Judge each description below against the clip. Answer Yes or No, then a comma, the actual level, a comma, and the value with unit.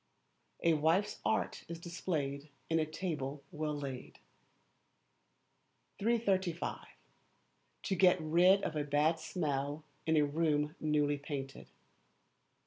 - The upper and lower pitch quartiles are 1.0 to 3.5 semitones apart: Yes, average, 3.0 semitones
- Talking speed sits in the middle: No, slow, 110 wpm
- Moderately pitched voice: Yes, medium, 155 Hz